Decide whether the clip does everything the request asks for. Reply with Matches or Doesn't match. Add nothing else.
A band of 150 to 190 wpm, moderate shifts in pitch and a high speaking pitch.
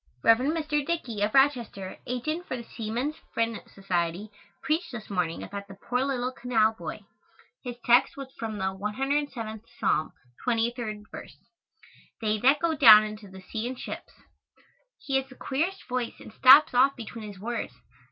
Matches